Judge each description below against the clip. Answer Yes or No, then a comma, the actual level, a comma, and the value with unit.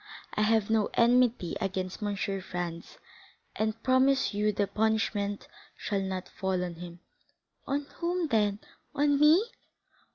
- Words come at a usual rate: No, slow, 125 wpm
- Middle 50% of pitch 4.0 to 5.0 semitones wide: Yes, average, 4.7 semitones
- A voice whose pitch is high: Yes, high, 210 Hz